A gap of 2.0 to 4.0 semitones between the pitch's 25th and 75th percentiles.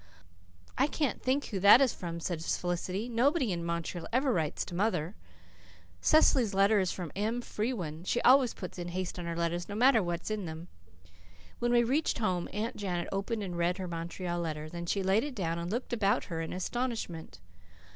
No: average, 5.2 semitones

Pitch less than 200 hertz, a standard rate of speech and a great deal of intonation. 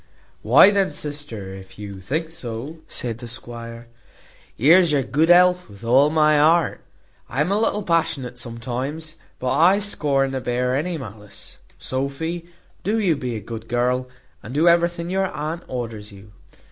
Yes: medium, 140 Hz; average, 160 wpm; wide, 6.0 semitones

